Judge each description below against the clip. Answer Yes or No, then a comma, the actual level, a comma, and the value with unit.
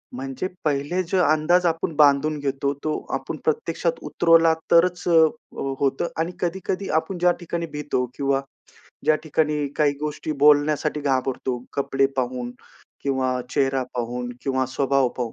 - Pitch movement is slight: No, average, 3.6 semitones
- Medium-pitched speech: Yes, medium, 145 Hz